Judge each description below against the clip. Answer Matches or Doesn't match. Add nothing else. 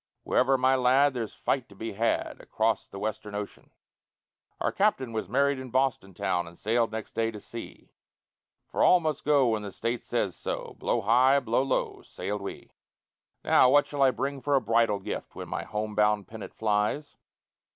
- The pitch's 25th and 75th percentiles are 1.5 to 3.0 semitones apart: Doesn't match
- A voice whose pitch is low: Matches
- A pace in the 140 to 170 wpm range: Doesn't match